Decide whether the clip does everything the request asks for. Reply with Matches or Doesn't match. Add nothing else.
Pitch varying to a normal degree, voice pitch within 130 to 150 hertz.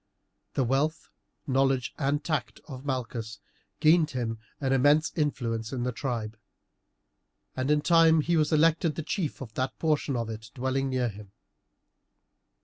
Matches